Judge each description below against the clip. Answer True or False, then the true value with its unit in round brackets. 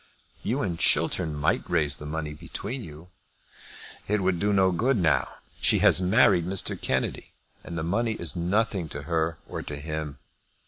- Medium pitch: False (85 Hz)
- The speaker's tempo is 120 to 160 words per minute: False (170 wpm)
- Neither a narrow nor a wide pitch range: True (3.9 semitones)